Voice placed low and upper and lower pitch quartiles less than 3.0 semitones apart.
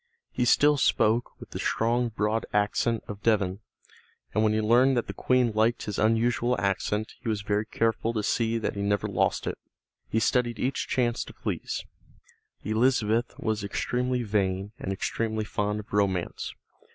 Yes: low, 110 Hz; narrow, 2.4 semitones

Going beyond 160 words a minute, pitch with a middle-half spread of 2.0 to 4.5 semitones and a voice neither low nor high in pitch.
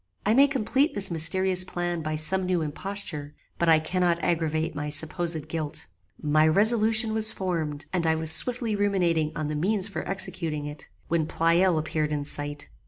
Yes: average, 170 wpm; average, 3.7 semitones; medium, 170 Hz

